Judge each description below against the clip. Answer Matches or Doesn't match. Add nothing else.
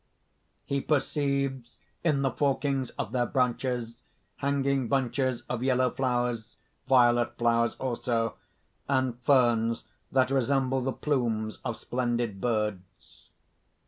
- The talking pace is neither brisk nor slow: Doesn't match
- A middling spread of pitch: Doesn't match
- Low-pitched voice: Matches